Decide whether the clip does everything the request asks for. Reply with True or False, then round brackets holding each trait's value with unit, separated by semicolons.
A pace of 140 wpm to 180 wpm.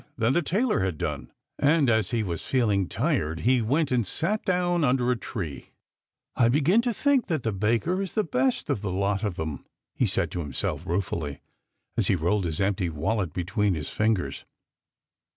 False (190 wpm)